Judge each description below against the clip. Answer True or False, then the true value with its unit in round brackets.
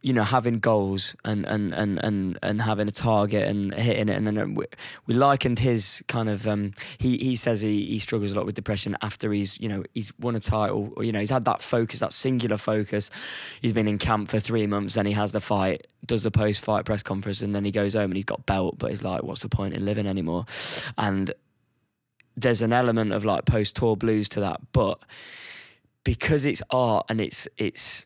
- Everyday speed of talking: False (225 wpm)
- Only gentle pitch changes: True (2.2 semitones)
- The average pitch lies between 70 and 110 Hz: True (105 Hz)